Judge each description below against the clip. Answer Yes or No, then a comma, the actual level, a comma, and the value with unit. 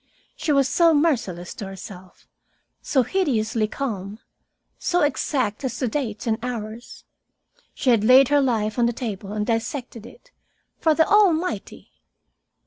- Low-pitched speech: No, high, 240 Hz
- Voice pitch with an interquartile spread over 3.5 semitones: Yes, average, 5.2 semitones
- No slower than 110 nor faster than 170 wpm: Yes, average, 140 wpm